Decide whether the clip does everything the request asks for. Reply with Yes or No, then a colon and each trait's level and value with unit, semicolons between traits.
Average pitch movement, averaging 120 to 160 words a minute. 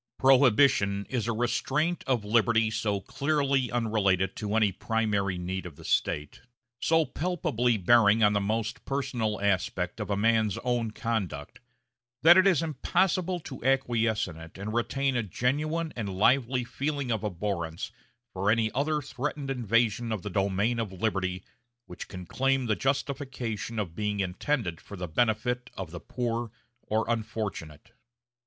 Yes: average, 4.6 semitones; average, 150 wpm